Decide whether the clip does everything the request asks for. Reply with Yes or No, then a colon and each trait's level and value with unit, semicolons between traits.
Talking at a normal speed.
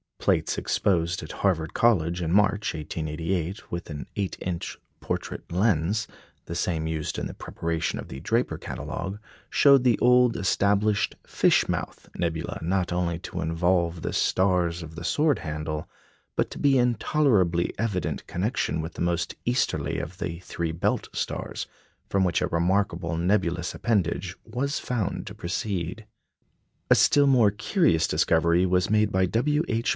Yes: average, 155 wpm